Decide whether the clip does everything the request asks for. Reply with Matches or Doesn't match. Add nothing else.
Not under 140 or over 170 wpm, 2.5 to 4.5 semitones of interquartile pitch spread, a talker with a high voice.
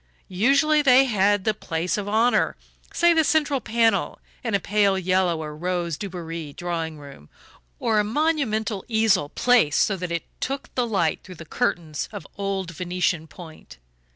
Doesn't match